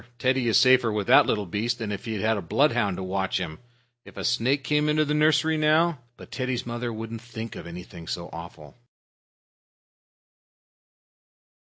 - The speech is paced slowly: No, average, 170 wpm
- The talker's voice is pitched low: Yes, low, 115 Hz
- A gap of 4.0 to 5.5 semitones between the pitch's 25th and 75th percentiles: Yes, average, 4.9 semitones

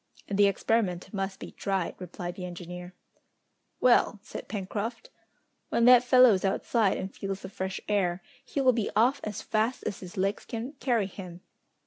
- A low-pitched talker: No, high, 200 Hz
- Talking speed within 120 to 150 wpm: No, average, 165 wpm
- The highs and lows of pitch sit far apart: No, average, 3.8 semitones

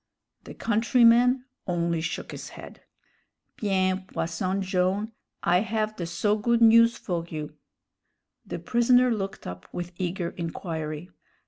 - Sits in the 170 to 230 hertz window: Yes, high, 190 Hz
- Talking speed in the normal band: No, slow, 125 wpm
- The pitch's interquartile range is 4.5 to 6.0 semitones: Yes, average, 4.9 semitones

